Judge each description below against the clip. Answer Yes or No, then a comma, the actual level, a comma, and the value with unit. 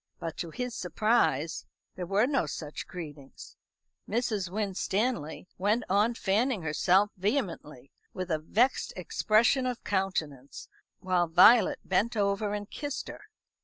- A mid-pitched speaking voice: No, high, 195 Hz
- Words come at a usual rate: No, slow, 130 wpm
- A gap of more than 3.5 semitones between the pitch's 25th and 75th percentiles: Yes, average, 5.0 semitones